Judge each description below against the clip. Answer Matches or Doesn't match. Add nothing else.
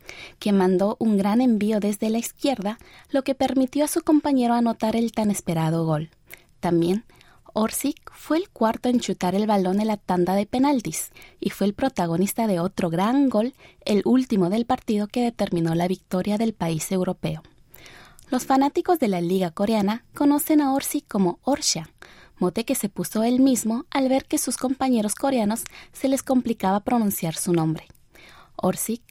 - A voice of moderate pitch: Doesn't match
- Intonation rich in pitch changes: Matches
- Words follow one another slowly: Doesn't match